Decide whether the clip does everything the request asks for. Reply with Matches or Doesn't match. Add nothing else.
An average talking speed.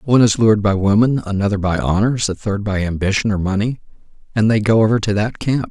Doesn't match